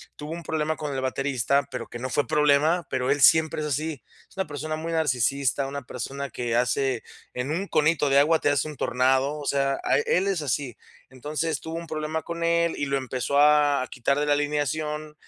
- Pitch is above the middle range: No, medium, 145 Hz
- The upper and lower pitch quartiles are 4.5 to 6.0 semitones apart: No, narrow, 2.5 semitones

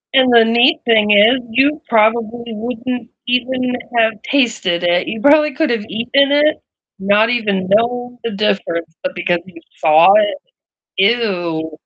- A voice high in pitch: Yes, high, 230 Hz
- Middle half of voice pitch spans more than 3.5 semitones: Yes, average, 4.1 semitones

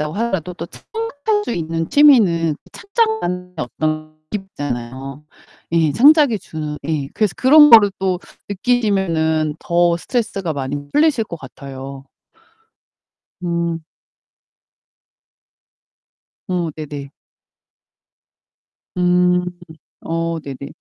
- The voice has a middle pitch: Yes, medium, 170 Hz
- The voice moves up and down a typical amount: No, wide, 5.7 semitones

